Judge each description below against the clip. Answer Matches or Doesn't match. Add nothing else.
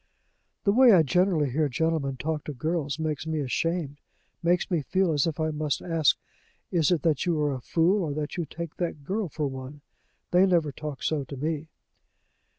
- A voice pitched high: Doesn't match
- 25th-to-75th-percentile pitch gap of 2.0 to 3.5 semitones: Matches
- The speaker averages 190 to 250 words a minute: Matches